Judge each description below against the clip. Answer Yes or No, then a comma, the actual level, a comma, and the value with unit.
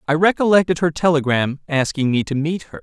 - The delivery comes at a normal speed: Yes, average, 190 wpm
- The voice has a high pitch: No, medium, 155 Hz